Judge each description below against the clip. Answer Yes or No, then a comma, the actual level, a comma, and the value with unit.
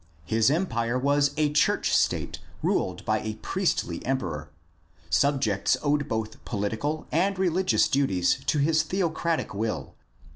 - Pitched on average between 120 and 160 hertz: Yes, medium, 140 Hz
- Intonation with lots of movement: Yes, wide, 6.3 semitones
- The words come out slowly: Yes, slow, 125 wpm